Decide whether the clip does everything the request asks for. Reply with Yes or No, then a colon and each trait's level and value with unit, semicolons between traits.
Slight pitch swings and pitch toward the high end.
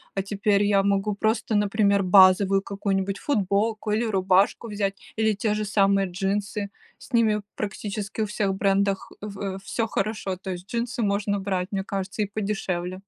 Yes: narrow, 1.5 semitones; high, 200 Hz